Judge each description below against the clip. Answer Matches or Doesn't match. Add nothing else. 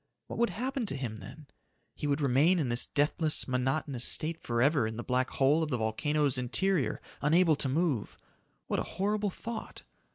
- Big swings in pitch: Doesn't match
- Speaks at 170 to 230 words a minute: Matches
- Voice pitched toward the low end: Doesn't match